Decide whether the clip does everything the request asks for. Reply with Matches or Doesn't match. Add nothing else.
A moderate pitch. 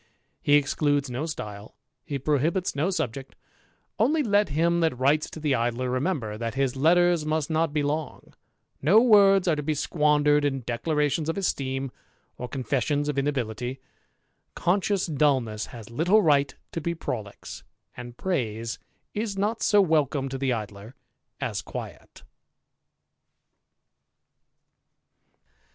Matches